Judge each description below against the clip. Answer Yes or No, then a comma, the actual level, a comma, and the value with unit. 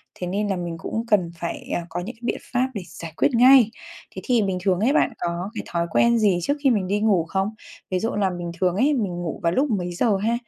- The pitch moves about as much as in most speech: Yes, average, 4.6 semitones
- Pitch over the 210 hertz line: No, high, 200 Hz